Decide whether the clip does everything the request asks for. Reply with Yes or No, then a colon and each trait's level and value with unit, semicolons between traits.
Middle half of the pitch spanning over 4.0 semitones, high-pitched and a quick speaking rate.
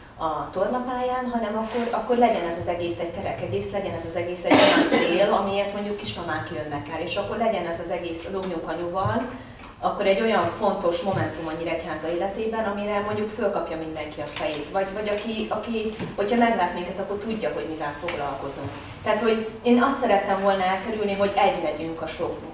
Yes: average, 4.6 semitones; high, 195 Hz; fast, 185 wpm